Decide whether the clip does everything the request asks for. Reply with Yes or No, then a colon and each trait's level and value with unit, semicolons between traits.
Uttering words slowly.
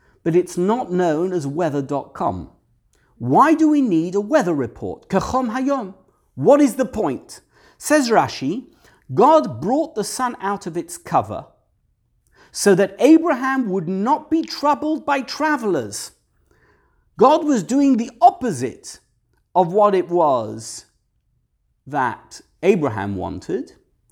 Yes: slow, 125 wpm